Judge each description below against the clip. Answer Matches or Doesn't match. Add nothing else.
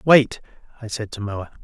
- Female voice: Doesn't match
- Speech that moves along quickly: Doesn't match